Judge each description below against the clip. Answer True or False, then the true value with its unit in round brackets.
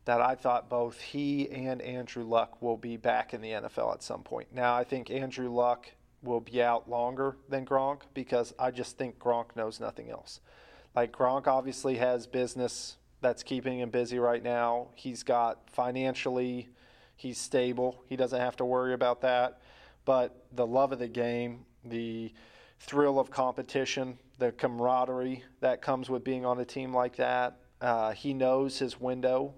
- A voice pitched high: False (125 Hz)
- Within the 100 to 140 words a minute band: False (170 wpm)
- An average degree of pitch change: False (1.3 semitones)